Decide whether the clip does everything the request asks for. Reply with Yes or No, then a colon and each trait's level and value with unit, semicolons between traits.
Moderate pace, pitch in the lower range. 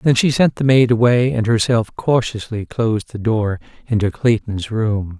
Yes: average, 175 wpm; low, 115 Hz